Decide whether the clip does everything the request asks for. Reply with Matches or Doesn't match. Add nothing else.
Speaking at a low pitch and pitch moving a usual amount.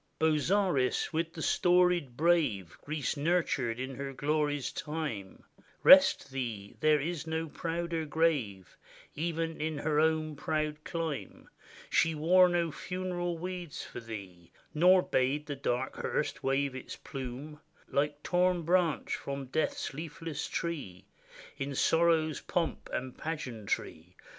Doesn't match